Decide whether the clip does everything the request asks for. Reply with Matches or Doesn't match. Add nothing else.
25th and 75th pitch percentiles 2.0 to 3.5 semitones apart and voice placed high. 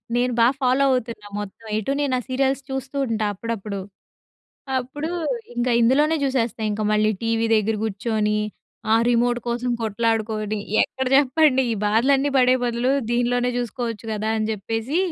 Matches